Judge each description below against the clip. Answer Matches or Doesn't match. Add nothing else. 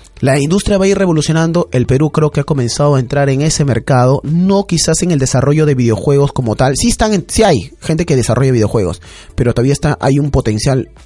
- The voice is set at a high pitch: Doesn't match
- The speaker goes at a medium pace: Doesn't match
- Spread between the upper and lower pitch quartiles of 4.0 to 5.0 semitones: Matches